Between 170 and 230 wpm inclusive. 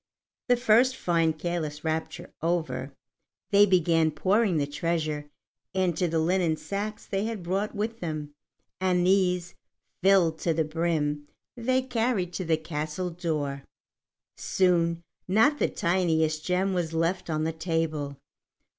No: slow, 135 wpm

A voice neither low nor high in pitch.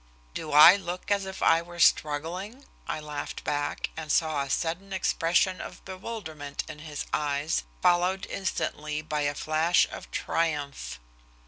Yes: medium, 160 Hz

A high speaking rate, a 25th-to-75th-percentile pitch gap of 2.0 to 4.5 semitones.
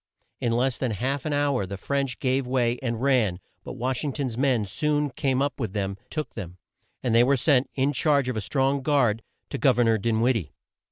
Yes: fast, 225 wpm; average, 3.4 semitones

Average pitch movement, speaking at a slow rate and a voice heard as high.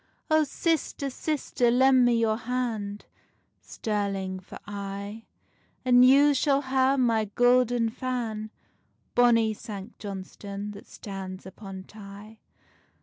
Yes: average, 3.9 semitones; slow, 110 wpm; high, 225 Hz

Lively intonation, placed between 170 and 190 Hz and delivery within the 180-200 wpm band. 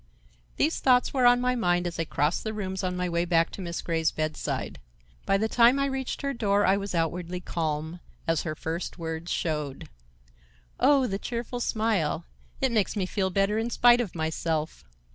Yes: wide, 6.0 semitones; medium, 185 Hz; average, 190 wpm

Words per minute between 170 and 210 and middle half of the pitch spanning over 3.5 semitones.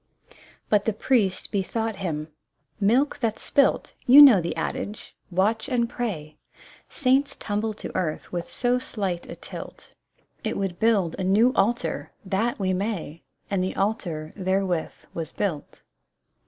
No: average, 160 wpm; average, 4.0 semitones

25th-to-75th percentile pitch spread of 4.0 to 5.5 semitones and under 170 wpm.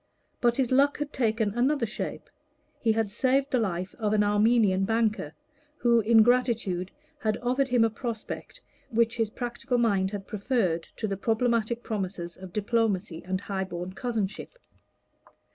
No: average, 3.5 semitones; average, 155 wpm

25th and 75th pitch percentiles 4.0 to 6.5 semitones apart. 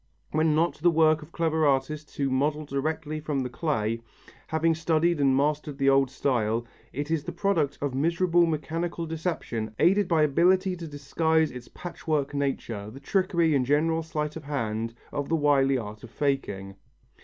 No: average, 3.2 semitones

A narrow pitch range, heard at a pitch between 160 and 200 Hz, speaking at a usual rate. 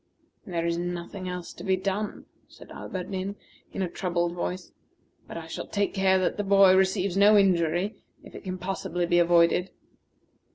Yes: narrow, 1.9 semitones; medium, 185 Hz; average, 170 wpm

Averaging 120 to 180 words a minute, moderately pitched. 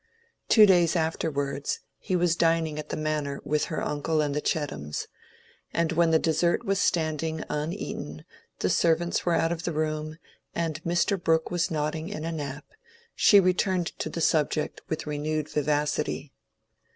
Yes: average, 160 wpm; medium, 160 Hz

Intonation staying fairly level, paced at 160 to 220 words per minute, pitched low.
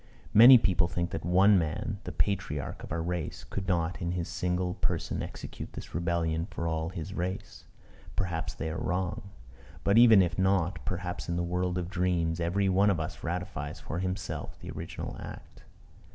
Yes: narrow, 2.0 semitones; average, 180 wpm; very low, 90 Hz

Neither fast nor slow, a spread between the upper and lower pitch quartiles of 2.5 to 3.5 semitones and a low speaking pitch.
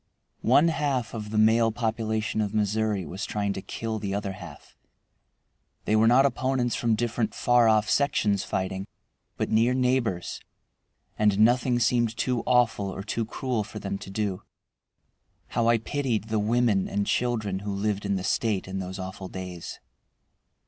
Yes: average, 160 wpm; average, 3.1 semitones; low, 110 Hz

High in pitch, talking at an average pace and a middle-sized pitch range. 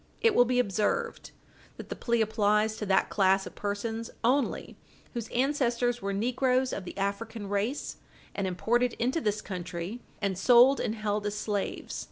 Yes: high, 220 Hz; average, 165 wpm; average, 3.3 semitones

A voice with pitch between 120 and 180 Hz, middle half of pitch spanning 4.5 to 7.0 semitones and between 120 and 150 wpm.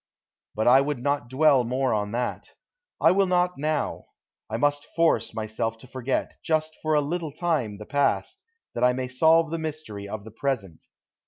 No: low, 135 Hz; average, 5.3 semitones; average, 180 wpm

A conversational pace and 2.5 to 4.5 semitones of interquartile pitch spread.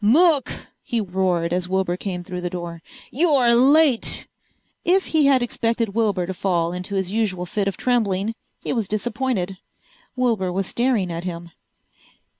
No: average, 155 wpm; average, 5.2 semitones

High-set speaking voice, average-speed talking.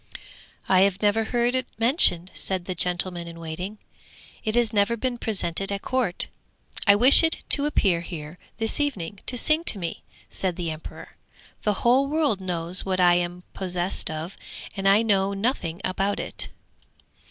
Yes: high, 195 Hz; average, 165 wpm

